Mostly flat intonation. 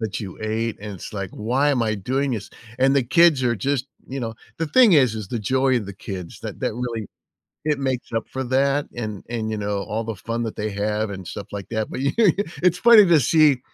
No: average, 4.3 semitones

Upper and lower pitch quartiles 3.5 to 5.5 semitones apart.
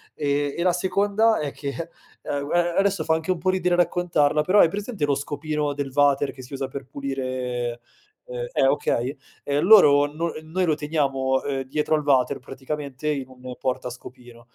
Yes: average, 4.1 semitones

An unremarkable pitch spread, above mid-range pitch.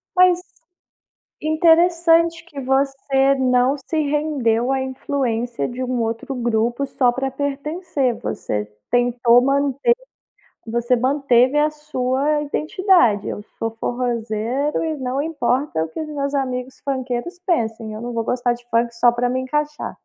Yes: average, 3.6 semitones; very high, 260 Hz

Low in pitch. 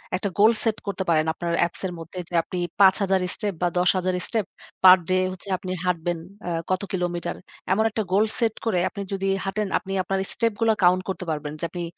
No: medium, 185 Hz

